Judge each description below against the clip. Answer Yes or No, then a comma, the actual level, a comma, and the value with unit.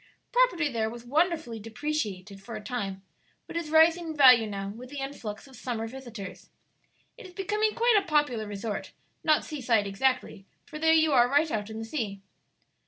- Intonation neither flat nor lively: No, wide, 6.4 semitones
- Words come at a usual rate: Yes, average, 185 wpm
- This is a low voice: No, very high, 255 Hz